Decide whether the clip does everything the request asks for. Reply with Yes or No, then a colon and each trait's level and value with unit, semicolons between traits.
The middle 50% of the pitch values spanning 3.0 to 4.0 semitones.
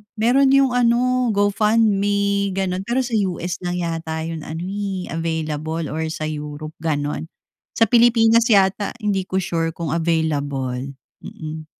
No: average, 4.9 semitones